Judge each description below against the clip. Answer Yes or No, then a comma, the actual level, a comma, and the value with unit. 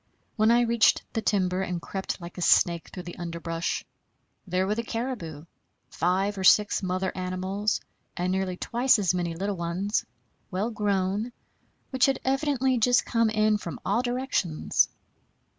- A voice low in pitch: No, high, 195 Hz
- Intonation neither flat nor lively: Yes, average, 4.1 semitones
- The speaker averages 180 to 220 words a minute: No, average, 155 wpm